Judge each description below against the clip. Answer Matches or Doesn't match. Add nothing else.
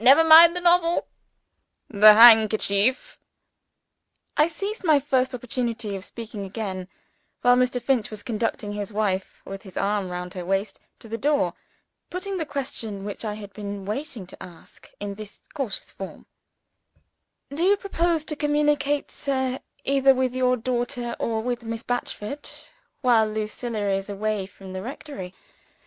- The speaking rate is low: Doesn't match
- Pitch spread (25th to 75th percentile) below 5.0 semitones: Doesn't match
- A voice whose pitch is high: Matches